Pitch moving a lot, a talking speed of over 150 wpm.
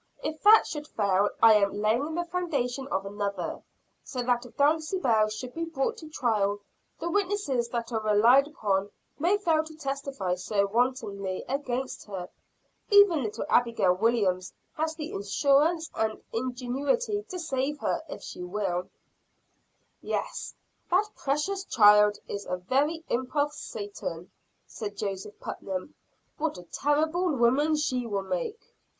No: wide, 7.0 semitones; average, 145 wpm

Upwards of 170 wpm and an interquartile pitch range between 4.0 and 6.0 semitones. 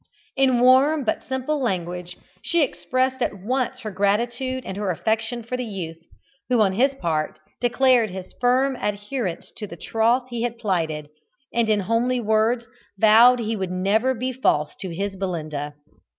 No: average, 165 wpm; average, 4.9 semitones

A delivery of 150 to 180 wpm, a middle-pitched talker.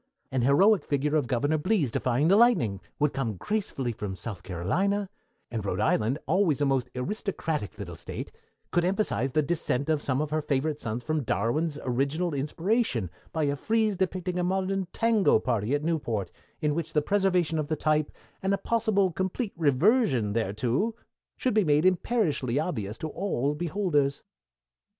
Yes: average, 165 wpm; medium, 150 Hz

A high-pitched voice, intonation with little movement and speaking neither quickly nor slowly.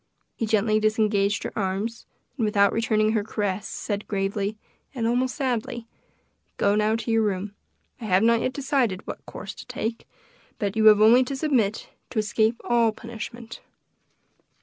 Yes: high, 220 Hz; narrow, 2.0 semitones; average, 160 wpm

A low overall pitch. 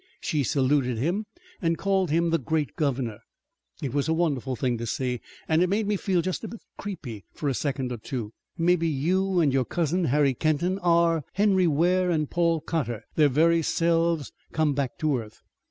No: medium, 160 Hz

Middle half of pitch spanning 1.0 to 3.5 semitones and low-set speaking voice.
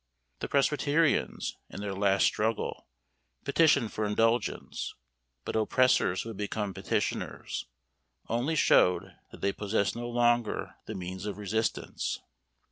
Yes: average, 3.2 semitones; low, 110 Hz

